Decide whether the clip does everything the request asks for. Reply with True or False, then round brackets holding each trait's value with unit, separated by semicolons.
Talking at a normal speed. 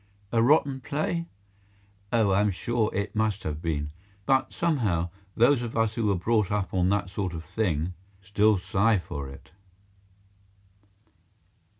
True (150 wpm)